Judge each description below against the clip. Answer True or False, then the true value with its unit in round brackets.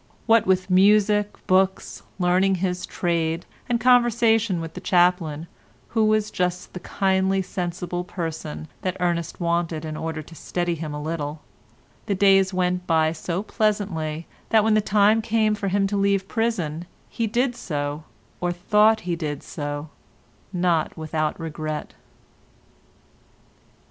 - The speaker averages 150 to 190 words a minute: False (140 wpm)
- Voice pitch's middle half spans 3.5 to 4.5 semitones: True (3.9 semitones)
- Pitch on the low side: False (180 Hz)